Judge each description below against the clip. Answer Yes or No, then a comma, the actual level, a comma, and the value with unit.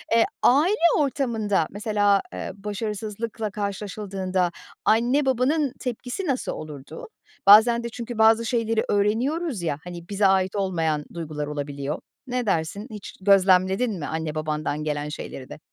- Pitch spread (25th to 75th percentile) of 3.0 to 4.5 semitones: No, wide, 5.5 semitones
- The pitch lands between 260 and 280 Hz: No, high, 205 Hz